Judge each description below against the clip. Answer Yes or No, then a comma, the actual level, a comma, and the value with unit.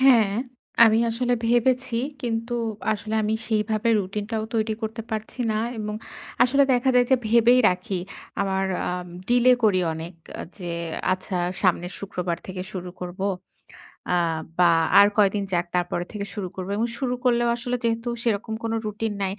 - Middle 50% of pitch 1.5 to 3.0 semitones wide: No, average, 3.9 semitones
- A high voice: Yes, high, 215 Hz